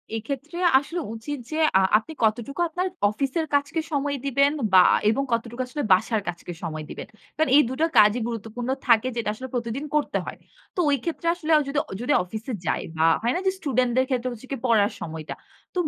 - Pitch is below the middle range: No, very high, 255 Hz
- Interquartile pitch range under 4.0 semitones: No, average, 4.5 semitones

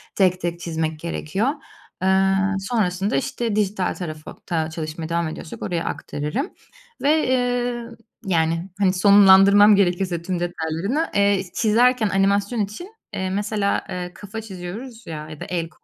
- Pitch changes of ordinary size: Yes, average, 3.7 semitones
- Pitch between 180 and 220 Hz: Yes, high, 190 Hz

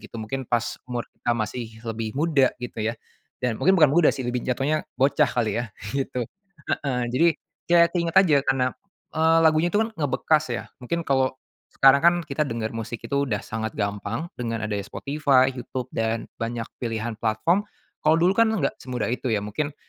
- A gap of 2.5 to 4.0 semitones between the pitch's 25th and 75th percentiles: No, average, 5.2 semitones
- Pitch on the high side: No, low, 130 Hz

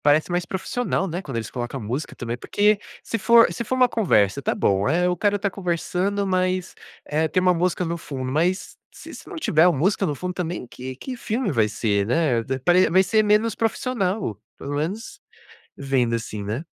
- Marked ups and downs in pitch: Yes, wide, 7.1 semitones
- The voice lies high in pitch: No, medium, 175 Hz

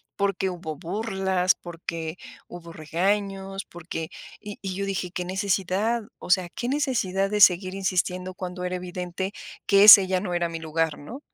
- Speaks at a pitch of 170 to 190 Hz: Yes, medium, 185 Hz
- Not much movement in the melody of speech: Yes, narrow, 2.0 semitones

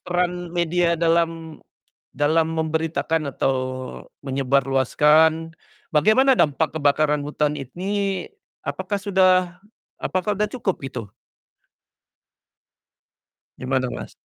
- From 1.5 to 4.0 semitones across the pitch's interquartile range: Yes, average, 3.5 semitones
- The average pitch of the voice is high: No, medium, 165 Hz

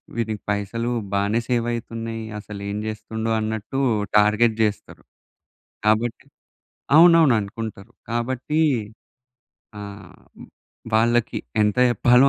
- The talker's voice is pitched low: Yes, low, 115 Hz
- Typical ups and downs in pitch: No, narrow, 2.2 semitones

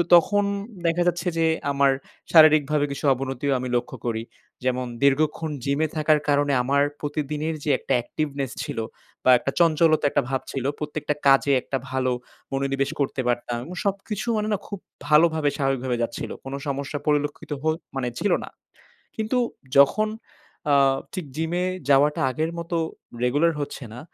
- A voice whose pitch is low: No, medium, 145 Hz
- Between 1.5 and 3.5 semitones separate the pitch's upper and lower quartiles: Yes, average, 3.0 semitones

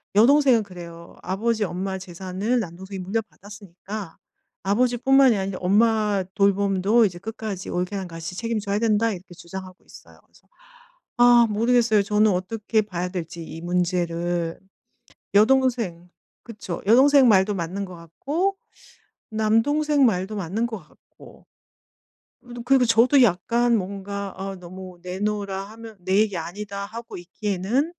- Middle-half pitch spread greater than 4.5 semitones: No, average, 3.8 semitones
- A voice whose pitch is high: Yes, high, 200 Hz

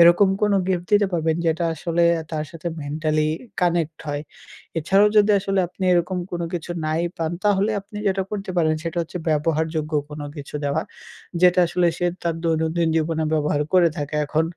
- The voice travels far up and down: No, narrow, 2.4 semitones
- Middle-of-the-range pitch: Yes, medium, 165 Hz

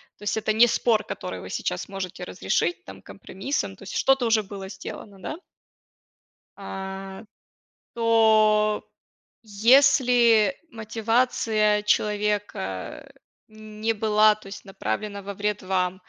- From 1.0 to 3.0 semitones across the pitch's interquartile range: Yes, narrow, 2.4 semitones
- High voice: Yes, high, 210 Hz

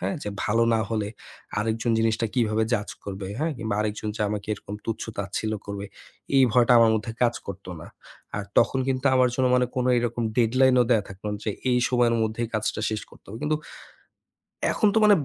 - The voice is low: Yes, low, 115 Hz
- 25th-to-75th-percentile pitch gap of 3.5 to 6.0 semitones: No, average, 2.7 semitones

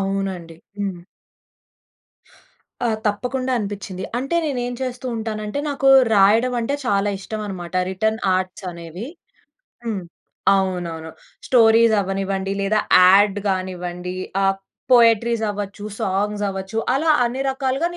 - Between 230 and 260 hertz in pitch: No, high, 205 Hz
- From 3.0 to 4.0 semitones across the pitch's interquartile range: Yes, average, 3.4 semitones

